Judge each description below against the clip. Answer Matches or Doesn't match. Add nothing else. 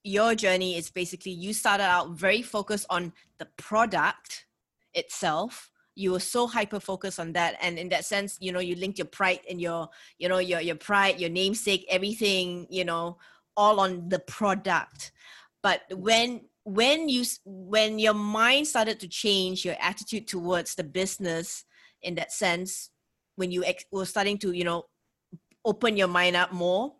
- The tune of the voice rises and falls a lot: Doesn't match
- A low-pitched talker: Doesn't match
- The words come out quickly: Doesn't match